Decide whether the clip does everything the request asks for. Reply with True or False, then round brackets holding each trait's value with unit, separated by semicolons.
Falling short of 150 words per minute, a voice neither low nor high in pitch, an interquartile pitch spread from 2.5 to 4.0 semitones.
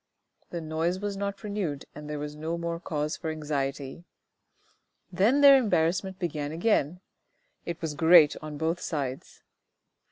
True (140 wpm; 165 Hz; 3.6 semitones)